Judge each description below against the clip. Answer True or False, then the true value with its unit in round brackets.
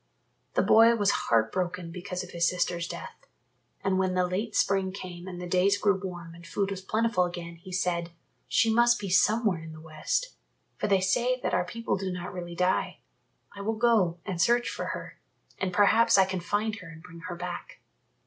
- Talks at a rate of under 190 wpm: False (205 wpm)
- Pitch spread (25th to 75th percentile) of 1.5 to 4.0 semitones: True (2.9 semitones)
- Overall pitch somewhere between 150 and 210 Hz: True (185 Hz)